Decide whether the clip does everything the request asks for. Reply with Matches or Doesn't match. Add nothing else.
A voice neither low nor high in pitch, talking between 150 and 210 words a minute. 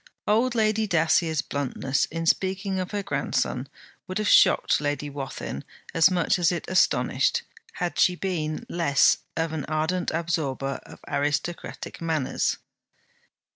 Doesn't match